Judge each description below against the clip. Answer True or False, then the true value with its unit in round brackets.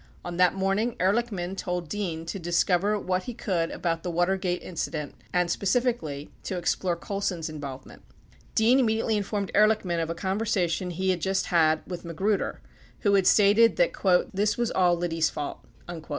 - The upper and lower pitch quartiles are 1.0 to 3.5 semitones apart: True (3.2 semitones)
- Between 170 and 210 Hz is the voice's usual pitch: True (185 Hz)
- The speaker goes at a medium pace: True (175 wpm)